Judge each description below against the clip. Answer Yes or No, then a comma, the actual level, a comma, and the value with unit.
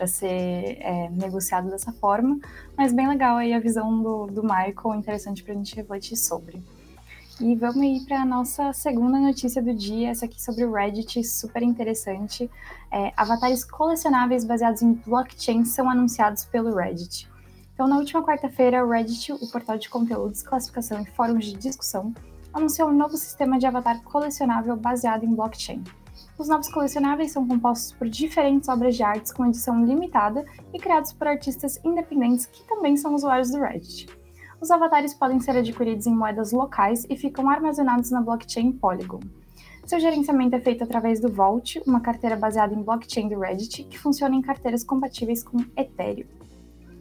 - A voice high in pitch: Yes, high, 240 Hz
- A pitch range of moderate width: Yes, average, 3.6 semitones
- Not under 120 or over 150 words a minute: No, average, 170 wpm